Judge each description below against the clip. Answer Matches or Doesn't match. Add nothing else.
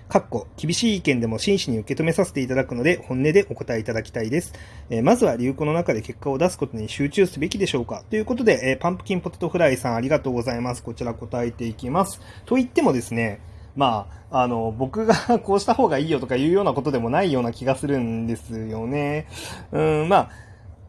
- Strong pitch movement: Matches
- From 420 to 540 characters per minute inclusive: Matches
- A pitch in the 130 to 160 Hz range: Matches